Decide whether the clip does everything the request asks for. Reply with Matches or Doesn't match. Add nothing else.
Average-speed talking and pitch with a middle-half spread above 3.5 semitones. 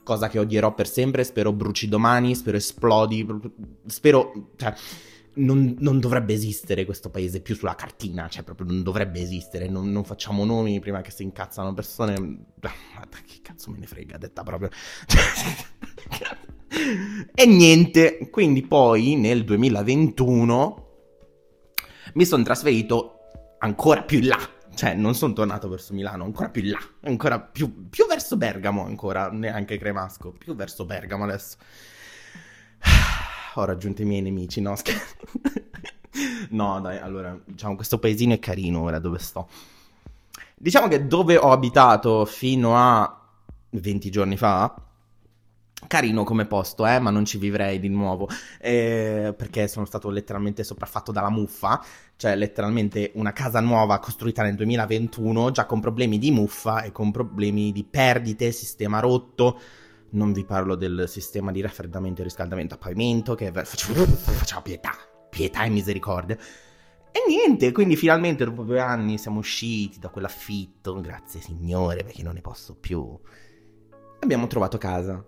Doesn't match